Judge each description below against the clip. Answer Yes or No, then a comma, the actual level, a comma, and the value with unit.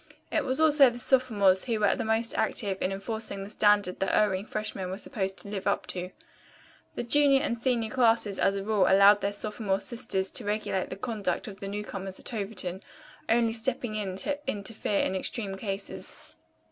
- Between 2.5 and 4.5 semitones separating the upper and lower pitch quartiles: Yes, average, 2.9 semitones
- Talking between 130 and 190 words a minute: Yes, average, 185 wpm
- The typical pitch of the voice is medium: No, high, 210 Hz